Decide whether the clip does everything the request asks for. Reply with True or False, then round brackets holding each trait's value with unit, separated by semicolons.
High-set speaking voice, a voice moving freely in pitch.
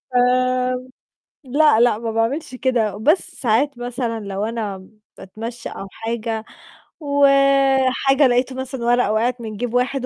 False (245 Hz; 2.8 semitones)